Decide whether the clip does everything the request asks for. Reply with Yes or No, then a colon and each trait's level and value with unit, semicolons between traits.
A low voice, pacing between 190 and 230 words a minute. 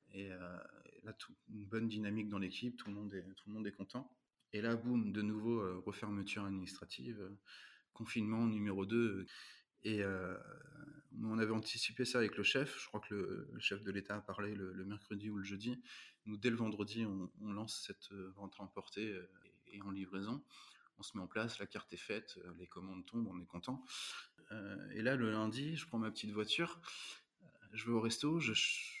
Yes: low, 105 Hz; average, 215 wpm